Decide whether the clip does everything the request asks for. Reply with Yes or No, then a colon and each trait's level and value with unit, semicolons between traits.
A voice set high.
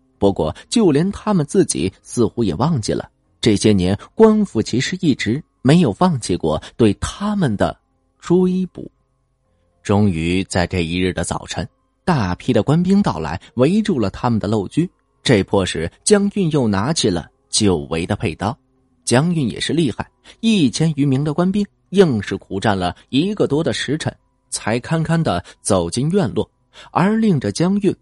No: low, 125 Hz